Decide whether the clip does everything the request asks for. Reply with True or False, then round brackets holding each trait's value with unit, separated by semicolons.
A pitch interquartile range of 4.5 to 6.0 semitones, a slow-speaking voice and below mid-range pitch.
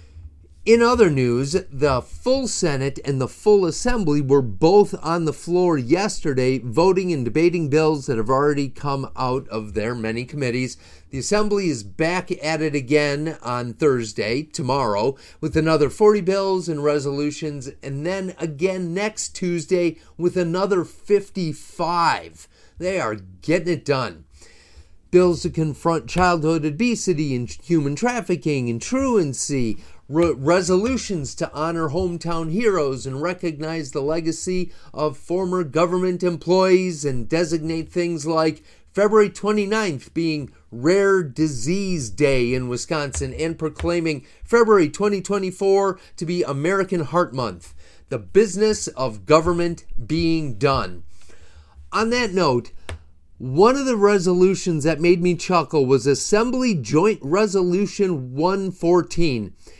False (5.1 semitones; 125 wpm; 165 Hz)